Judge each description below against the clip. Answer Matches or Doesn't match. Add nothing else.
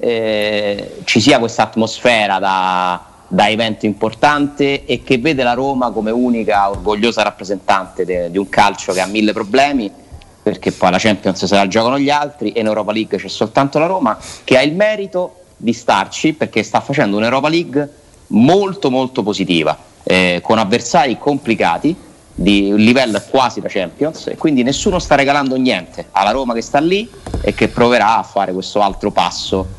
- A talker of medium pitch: Doesn't match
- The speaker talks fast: Matches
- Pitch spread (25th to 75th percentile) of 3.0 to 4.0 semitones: Doesn't match